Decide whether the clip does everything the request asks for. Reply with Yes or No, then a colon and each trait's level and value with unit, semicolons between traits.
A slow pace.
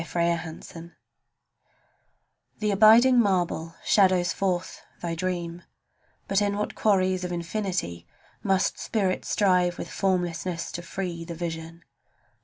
Yes: slow, 115 wpm